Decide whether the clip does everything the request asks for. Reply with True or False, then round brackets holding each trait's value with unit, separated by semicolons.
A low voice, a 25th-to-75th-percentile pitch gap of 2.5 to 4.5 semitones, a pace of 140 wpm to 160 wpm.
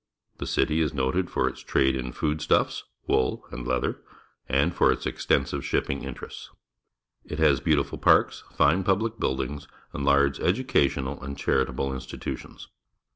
True (70 Hz; 2.8 semitones; 145 wpm)